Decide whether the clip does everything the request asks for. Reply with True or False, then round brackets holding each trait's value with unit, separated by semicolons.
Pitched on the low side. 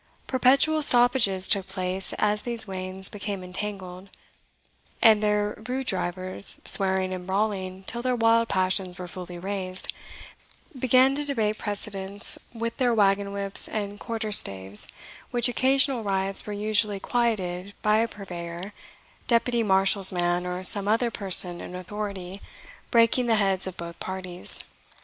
False (200 Hz)